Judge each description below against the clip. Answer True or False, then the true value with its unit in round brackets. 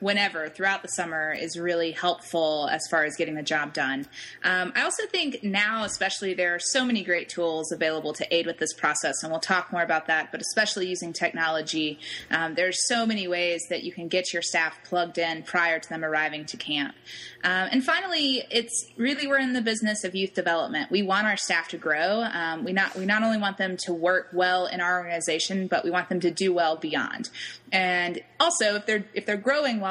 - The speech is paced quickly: True (220 wpm)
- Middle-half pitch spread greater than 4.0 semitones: False (3.5 semitones)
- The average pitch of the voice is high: False (180 Hz)